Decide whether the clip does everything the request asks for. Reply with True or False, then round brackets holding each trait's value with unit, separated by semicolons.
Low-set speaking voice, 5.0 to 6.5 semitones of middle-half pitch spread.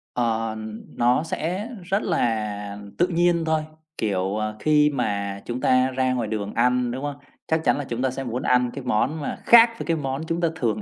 True (125 Hz; 5.6 semitones)